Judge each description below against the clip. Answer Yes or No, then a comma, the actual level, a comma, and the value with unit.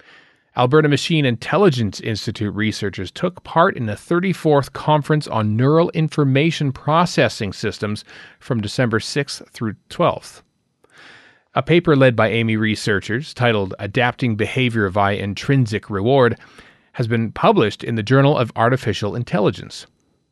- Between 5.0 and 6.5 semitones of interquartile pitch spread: Yes, wide, 5.4 semitones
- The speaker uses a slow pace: Yes, slow, 125 wpm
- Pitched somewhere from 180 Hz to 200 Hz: No, low, 120 Hz